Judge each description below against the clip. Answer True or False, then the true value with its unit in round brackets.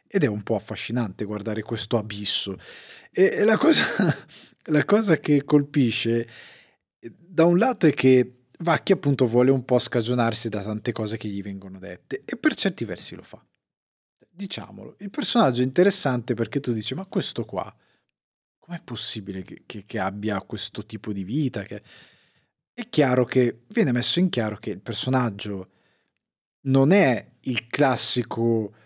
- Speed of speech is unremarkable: True (155 wpm)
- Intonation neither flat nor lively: False (6.4 semitones)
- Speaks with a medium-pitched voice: False (125 Hz)